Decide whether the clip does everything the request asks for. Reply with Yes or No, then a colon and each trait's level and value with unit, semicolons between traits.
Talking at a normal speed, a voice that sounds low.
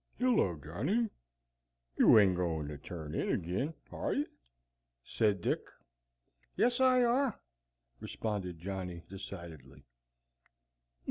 No: slow, 105 wpm; very low, 95 Hz